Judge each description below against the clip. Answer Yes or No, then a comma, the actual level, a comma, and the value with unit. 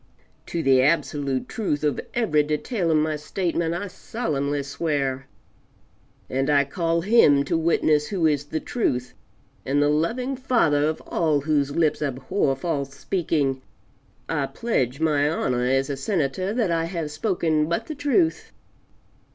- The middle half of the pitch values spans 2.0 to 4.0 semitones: Yes, average, 3.3 semitones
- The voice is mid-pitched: Yes, medium, 155 Hz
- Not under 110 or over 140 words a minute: No, average, 150 wpm